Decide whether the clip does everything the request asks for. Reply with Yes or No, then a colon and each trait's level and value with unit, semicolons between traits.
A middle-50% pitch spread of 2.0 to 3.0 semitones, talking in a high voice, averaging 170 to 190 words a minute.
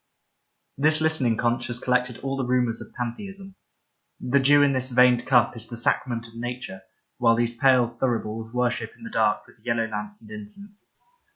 No: narrow, 2.5 semitones; low, 120 Hz; average, 180 wpm